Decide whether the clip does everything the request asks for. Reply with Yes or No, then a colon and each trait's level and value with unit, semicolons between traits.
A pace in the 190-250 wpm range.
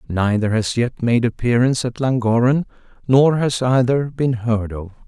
No: average, 155 wpm